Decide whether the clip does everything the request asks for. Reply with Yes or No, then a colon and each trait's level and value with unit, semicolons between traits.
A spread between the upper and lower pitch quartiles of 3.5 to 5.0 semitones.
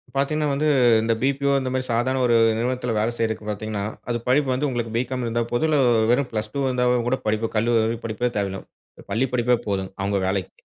No: average, 3.0 semitones